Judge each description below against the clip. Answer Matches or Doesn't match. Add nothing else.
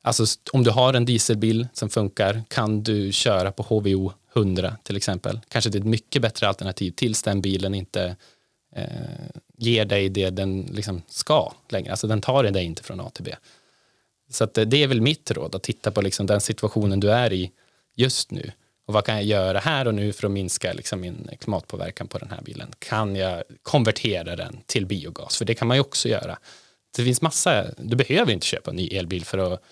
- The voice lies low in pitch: Matches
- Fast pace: Matches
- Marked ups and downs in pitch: Doesn't match